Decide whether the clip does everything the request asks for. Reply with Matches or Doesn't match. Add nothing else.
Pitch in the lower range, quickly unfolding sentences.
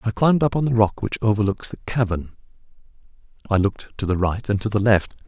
Matches